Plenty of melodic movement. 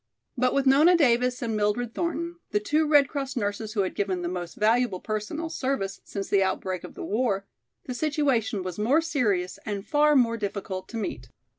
Yes: wide, 5.7 semitones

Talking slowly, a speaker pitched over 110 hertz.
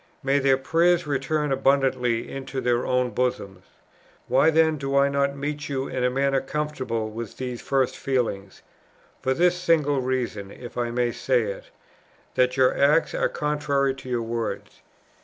No: average, 160 wpm; low, 135 Hz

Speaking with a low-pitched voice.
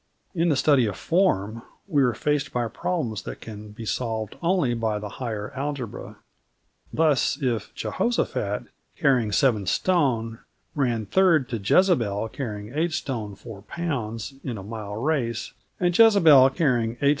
Yes: low, 125 Hz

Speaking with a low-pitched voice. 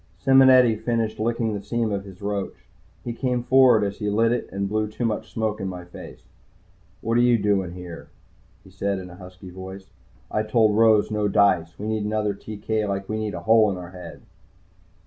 Yes: low, 105 Hz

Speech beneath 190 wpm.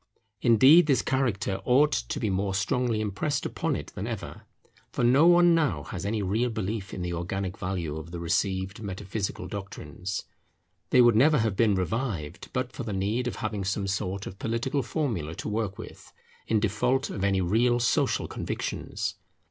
Yes: average, 175 wpm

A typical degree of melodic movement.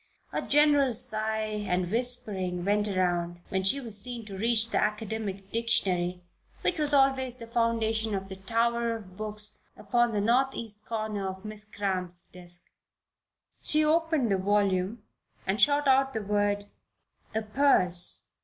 Yes: average, 3.5 semitones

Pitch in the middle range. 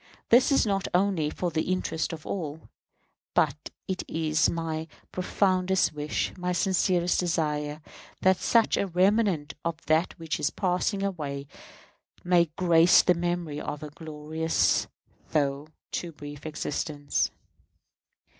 Yes: medium, 165 Hz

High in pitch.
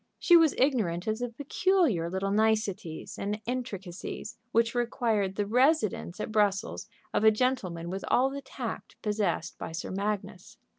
Yes: high, 215 Hz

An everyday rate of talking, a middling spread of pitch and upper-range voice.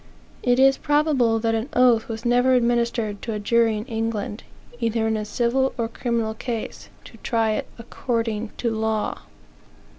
No: average, 160 wpm; narrow, 1.7 semitones; high, 230 Hz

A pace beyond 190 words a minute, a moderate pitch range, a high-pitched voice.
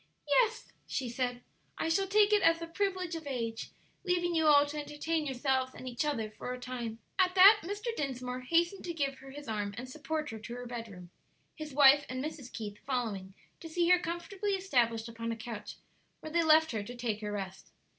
No: fast, 205 wpm; wide, 5.9 semitones; very high, 275 Hz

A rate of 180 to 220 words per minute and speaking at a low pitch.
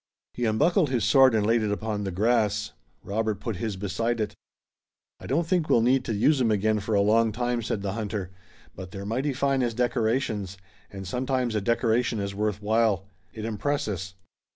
Yes: average, 190 wpm; low, 110 Hz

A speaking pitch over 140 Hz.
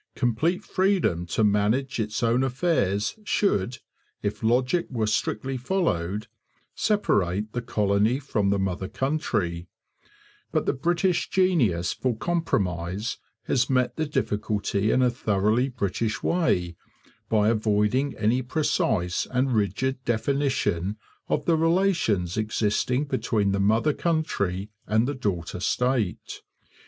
No: low, 115 Hz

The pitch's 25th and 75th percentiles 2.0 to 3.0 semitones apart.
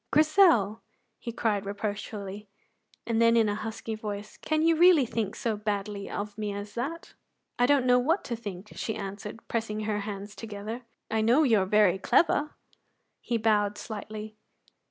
Yes: narrow, 2.4 semitones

